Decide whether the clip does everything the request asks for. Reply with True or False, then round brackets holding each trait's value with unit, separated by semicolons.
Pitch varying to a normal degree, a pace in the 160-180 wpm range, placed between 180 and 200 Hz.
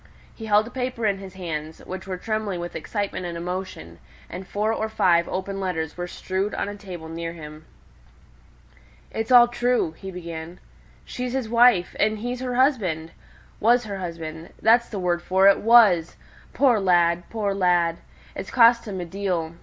True (4.4 semitones; 175 wpm; 190 Hz)